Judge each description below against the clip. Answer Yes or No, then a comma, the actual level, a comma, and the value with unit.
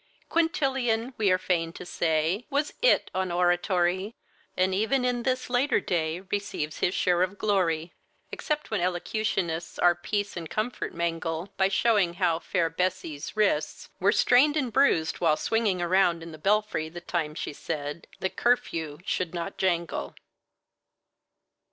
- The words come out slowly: No, average, 150 wpm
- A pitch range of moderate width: Yes, average, 4.4 semitones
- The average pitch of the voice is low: No, medium, 185 Hz